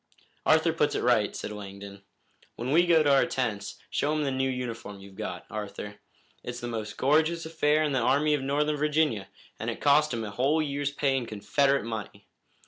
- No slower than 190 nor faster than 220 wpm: Yes, average, 200 wpm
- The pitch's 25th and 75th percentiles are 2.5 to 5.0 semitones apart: No, wide, 5.5 semitones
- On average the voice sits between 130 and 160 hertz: Yes, low, 135 Hz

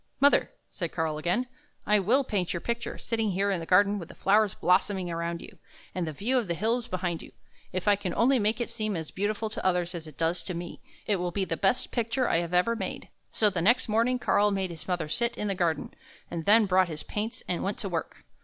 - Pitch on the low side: No, high, 195 Hz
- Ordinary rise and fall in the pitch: Yes, average, 4.1 semitones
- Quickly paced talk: Yes, fast, 250 wpm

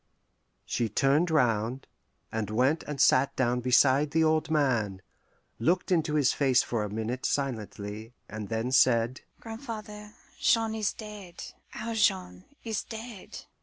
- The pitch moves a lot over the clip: Yes, wide, 7.9 semitones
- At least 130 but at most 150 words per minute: Yes, average, 140 wpm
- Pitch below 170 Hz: Yes, low, 135 Hz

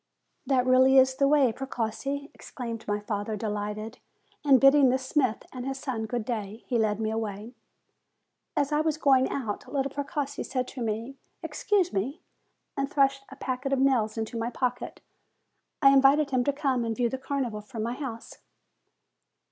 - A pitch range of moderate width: Yes, average, 3.5 semitones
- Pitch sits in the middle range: No, very high, 255 Hz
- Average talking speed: Yes, average, 170 wpm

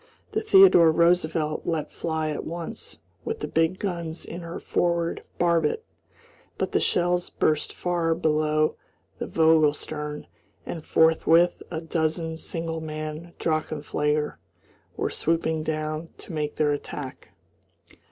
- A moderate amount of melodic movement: No, narrow, 1.7 semitones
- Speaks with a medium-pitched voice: Yes, medium, 160 Hz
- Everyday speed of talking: No, slow, 125 wpm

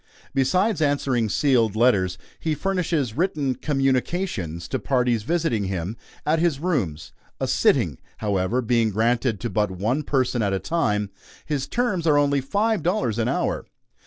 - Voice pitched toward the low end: Yes, low, 130 Hz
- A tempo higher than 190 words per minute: No, average, 150 wpm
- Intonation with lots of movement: Yes, wide, 6.3 semitones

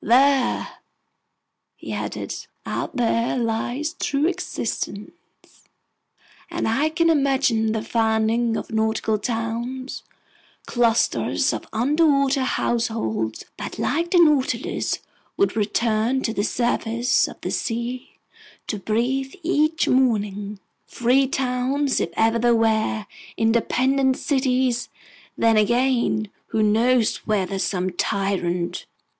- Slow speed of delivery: Yes, slow, 105 wpm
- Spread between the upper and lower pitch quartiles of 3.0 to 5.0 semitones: Yes, average, 3.3 semitones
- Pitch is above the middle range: Yes, high, 235 Hz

